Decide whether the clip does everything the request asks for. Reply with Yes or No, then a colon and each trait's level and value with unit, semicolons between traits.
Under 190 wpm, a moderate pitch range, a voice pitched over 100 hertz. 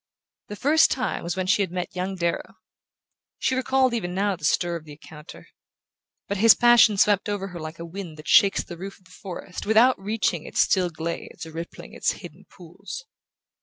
No: average, 200 wpm; average, 3.7 semitones; high, 190 Hz